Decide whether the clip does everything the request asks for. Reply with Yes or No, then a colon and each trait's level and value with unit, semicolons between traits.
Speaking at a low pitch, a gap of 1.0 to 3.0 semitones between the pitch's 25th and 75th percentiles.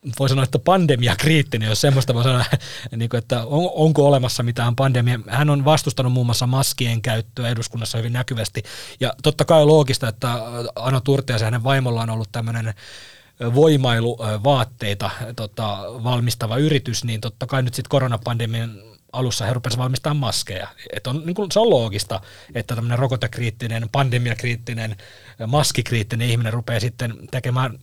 Yes: low, 120 Hz; narrow, 2.6 semitones